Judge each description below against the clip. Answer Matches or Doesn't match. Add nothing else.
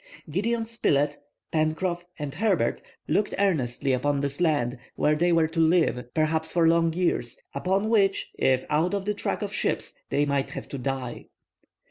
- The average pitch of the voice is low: Doesn't match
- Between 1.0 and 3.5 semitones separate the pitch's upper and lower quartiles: Doesn't match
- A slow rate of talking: Doesn't match